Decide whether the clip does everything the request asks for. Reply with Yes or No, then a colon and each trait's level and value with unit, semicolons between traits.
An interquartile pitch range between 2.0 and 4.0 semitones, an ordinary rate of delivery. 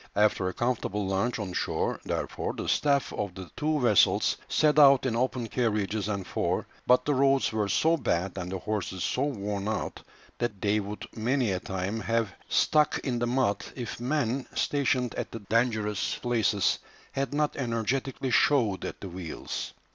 No: average, 4.5 semitones; average, 170 wpm